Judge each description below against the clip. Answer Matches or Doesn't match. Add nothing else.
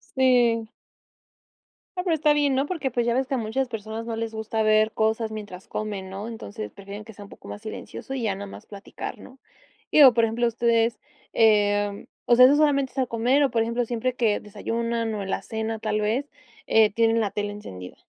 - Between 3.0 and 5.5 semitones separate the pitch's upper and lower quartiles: Doesn't match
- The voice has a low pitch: Doesn't match